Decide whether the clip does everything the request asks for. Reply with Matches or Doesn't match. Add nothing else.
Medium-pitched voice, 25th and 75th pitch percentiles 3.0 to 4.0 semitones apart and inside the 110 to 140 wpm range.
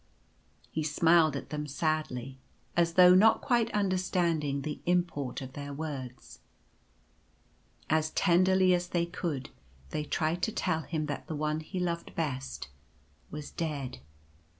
Matches